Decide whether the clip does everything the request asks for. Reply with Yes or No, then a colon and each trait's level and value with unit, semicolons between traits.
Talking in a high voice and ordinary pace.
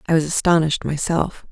No: medium, 160 Hz; average, 160 wpm